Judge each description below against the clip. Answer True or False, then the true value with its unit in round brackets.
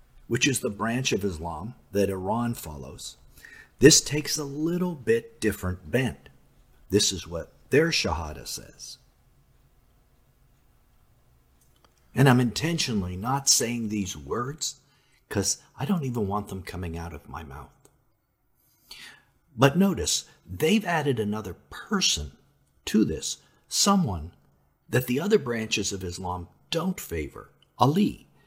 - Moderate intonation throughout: False (8.1 semitones)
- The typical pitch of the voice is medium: False (115 Hz)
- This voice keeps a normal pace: False (120 wpm)